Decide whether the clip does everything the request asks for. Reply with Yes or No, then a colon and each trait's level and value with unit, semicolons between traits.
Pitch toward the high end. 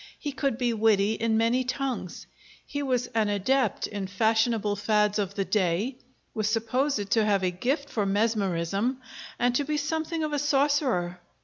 Yes: high, 225 Hz